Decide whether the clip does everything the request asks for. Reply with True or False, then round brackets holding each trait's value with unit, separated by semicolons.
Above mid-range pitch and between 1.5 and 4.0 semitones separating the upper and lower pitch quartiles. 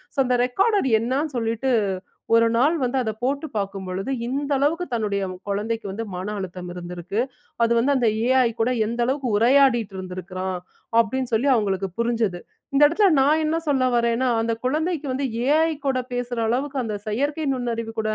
False (240 Hz; 4.4 semitones)